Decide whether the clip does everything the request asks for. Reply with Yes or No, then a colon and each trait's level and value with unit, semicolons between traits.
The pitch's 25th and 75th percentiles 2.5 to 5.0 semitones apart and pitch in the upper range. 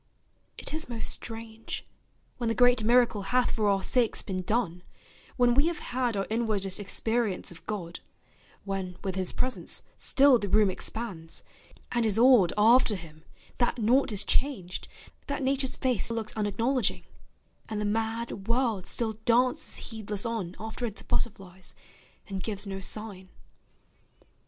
Yes: average, 3.7 semitones; high, 220 Hz